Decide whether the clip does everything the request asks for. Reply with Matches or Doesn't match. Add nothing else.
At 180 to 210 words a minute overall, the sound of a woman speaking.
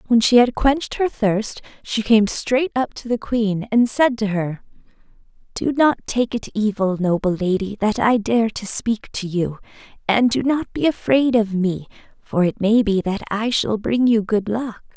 Matches